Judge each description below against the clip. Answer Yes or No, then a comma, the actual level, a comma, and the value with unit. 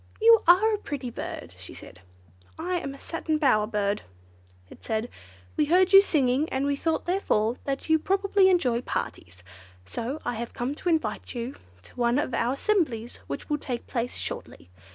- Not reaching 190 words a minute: Yes, average, 180 wpm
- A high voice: Yes, very high, 275 Hz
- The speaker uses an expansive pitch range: Yes, wide, 6.6 semitones